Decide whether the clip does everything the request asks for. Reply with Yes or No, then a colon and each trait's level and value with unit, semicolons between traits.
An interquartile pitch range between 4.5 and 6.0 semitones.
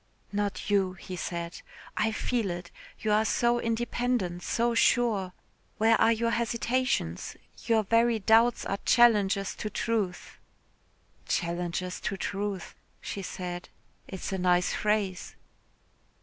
No: average, 3.9 semitones